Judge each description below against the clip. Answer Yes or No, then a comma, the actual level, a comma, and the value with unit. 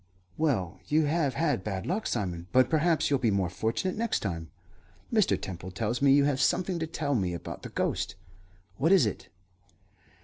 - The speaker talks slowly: No, average, 180 wpm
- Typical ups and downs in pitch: No, wide, 8.7 semitones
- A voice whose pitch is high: No, low, 130 Hz